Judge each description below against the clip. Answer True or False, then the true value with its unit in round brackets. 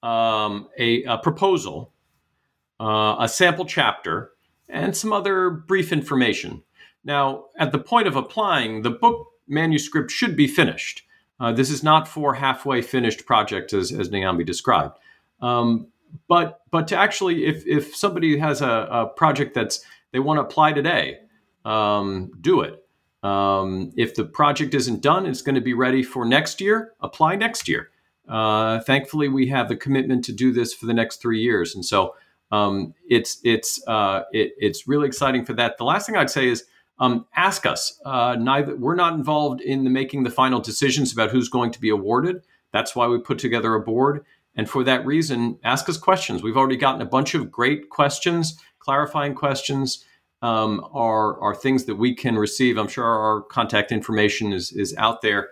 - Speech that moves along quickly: False (180 wpm)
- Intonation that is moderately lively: True (4.4 semitones)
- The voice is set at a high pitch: False (130 Hz)